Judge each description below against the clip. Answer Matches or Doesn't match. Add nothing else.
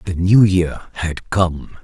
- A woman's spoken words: Doesn't match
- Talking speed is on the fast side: Doesn't match